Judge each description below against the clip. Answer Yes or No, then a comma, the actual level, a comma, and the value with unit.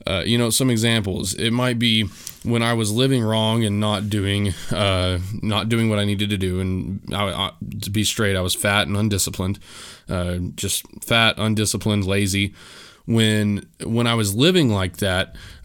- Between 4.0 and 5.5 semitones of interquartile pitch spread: No, narrow, 2.6 semitones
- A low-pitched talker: Yes, low, 105 Hz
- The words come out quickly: No, average, 180 wpm